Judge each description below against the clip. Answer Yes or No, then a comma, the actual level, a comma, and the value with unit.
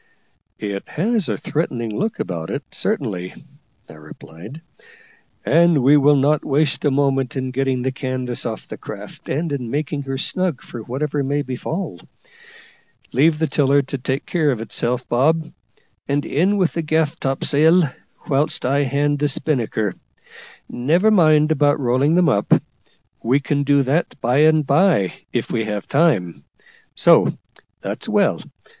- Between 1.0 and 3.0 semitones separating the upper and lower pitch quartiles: No, average, 3.5 semitones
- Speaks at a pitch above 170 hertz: No, medium, 140 Hz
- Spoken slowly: No, average, 150 wpm